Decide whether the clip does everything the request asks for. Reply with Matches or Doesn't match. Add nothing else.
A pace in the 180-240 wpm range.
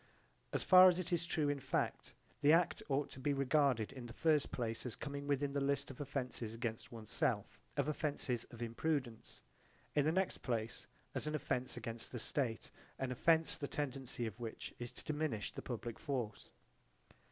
Matches